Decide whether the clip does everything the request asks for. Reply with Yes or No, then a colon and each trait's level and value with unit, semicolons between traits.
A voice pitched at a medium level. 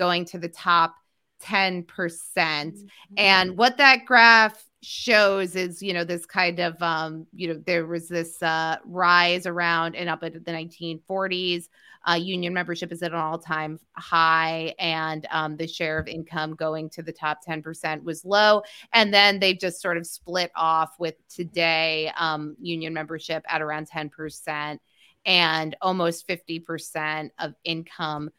Yes: medium, 170 Hz